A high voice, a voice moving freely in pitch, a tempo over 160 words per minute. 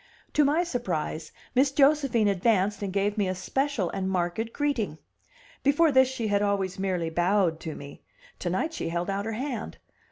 Yes: high, 205 Hz; wide, 6.2 semitones; average, 180 wpm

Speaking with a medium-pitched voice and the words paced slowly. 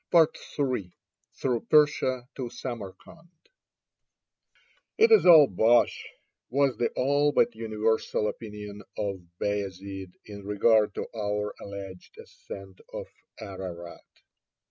No: low, 105 Hz; slow, 100 wpm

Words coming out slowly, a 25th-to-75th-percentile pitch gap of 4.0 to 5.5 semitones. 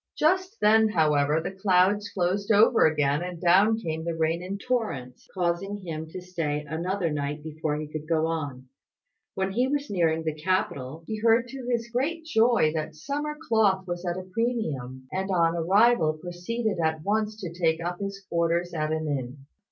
No: average, 180 wpm; average, 5.1 semitones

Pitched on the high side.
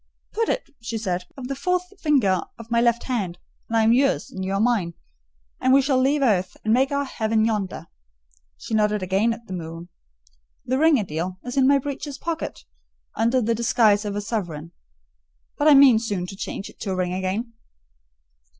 Yes: high, 225 Hz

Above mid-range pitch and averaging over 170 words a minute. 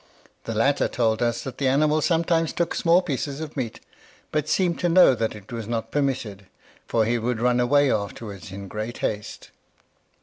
No: low, 125 Hz; average, 180 wpm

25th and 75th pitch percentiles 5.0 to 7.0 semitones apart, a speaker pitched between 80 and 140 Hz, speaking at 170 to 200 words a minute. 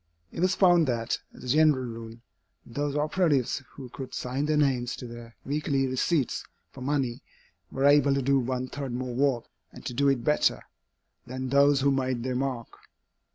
No: narrow, 2.4 semitones; low, 135 Hz; average, 180 wpm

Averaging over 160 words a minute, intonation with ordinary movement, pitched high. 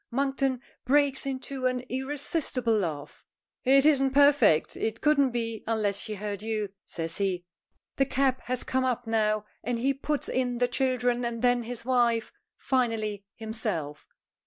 No: average, 150 wpm; average, 3.6 semitones; high, 245 Hz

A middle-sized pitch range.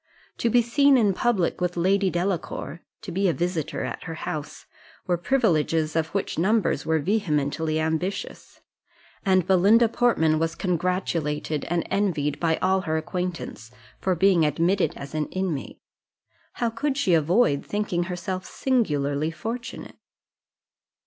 Yes: average, 3.9 semitones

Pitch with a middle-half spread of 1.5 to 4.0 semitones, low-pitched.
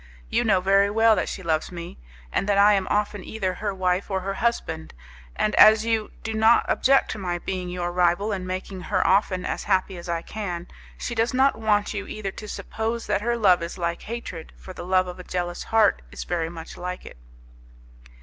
No: average, 3.2 semitones; high, 195 Hz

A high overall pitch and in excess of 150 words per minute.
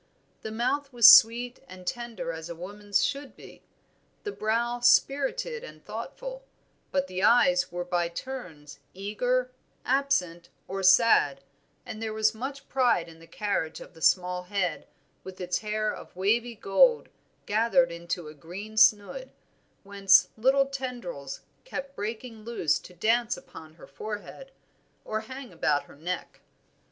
No: high, 215 Hz; average, 145 wpm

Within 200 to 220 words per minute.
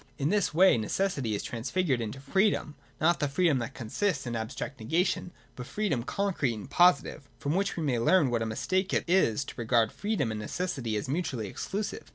Yes: fast, 205 wpm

